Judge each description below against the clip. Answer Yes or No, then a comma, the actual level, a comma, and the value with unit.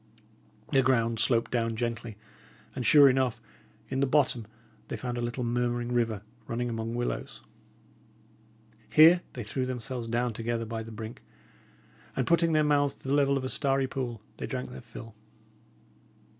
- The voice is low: Yes, low, 120 Hz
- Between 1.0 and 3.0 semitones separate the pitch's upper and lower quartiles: Yes, average, 2.7 semitones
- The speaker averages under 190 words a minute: Yes, average, 160 wpm